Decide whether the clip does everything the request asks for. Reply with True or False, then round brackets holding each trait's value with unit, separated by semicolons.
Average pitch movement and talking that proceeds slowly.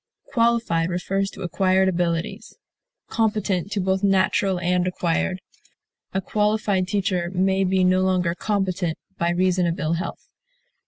False (1.7 semitones; 130 wpm)